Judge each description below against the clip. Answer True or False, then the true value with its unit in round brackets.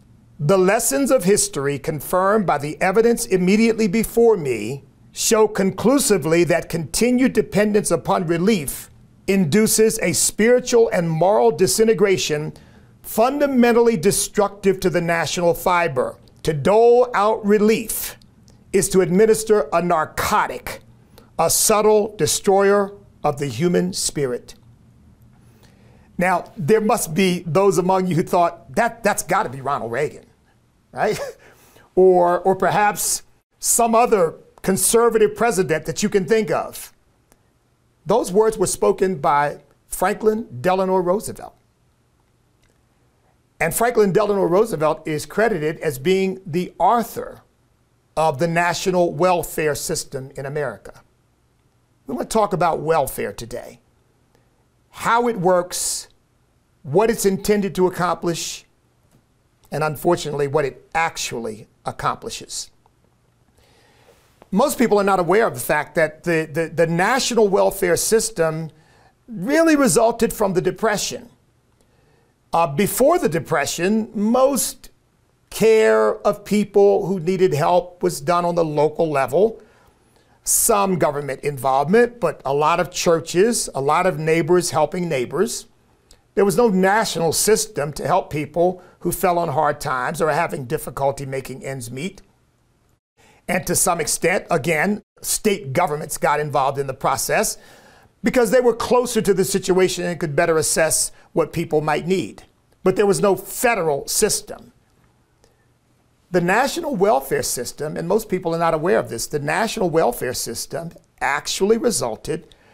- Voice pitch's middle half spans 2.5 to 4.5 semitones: False (5.2 semitones)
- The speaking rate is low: True (130 wpm)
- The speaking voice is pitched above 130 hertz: True (185 Hz)